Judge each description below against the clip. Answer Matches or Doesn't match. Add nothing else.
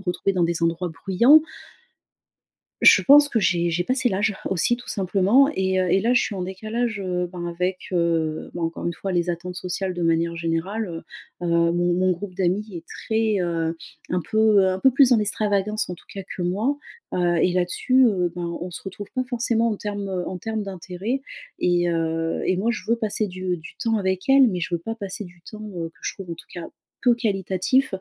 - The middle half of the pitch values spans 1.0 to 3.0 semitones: Doesn't match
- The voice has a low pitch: Doesn't match